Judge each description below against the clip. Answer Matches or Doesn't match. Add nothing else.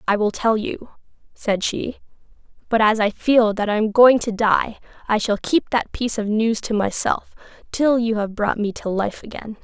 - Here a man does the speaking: Doesn't match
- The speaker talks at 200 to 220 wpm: Matches